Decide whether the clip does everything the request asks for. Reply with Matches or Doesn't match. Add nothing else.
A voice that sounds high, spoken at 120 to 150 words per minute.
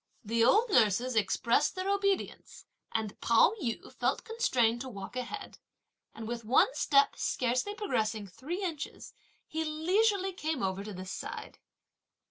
Matches